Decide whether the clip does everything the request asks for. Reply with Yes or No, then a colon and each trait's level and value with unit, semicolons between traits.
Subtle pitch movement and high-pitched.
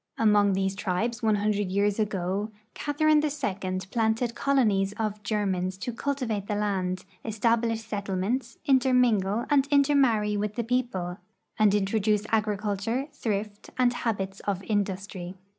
No: average, 3.2 semitones; high, 210 Hz